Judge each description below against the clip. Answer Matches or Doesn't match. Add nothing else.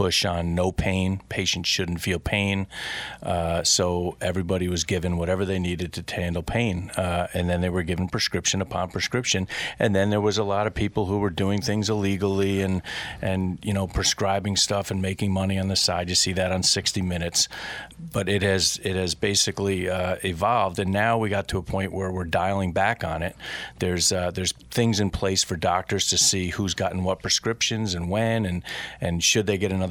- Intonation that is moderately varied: Doesn't match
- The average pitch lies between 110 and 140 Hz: Doesn't match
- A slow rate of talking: Doesn't match